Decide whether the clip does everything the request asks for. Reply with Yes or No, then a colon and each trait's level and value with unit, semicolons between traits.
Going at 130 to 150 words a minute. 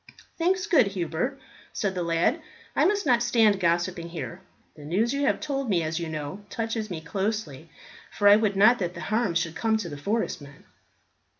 No: average, 190 wpm